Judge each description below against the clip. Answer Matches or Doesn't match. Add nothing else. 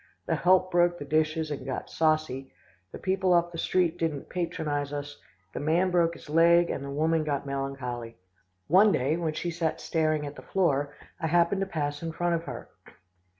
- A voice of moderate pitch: Matches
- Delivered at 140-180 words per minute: Doesn't match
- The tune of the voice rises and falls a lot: Doesn't match